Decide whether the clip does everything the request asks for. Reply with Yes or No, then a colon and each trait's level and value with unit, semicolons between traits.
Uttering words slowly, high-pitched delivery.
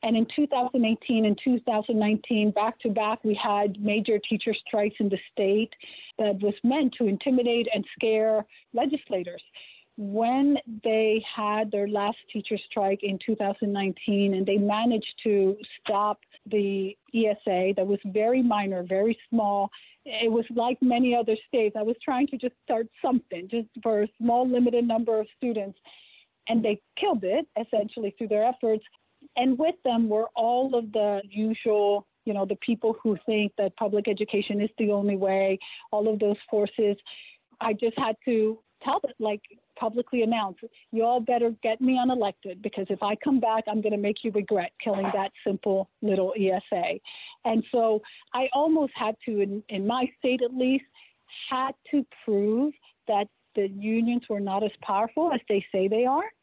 No: average, 165 wpm; high, 220 Hz